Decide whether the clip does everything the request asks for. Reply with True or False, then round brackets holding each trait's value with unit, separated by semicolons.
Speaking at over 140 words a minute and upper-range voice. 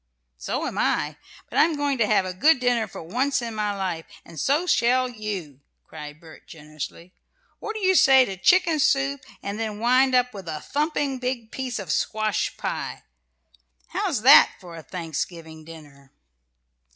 True (170 wpm; 215 Hz)